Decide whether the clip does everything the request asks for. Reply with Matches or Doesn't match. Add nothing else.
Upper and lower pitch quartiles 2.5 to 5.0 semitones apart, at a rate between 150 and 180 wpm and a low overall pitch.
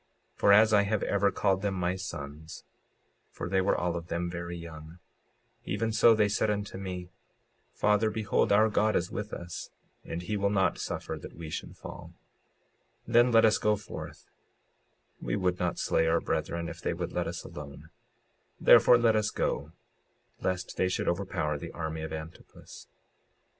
Matches